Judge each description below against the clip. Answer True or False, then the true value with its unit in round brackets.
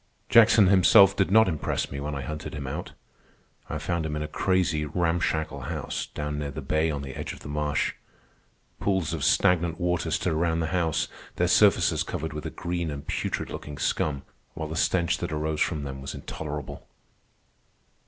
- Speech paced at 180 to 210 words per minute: True (185 wpm)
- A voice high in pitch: False (80 Hz)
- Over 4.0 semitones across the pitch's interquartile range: False (2.8 semitones)